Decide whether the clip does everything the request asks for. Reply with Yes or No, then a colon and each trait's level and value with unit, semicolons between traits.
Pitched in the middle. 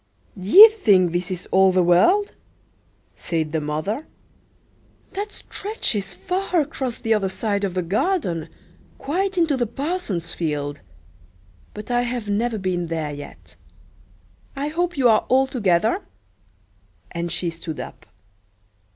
No: high, 205 Hz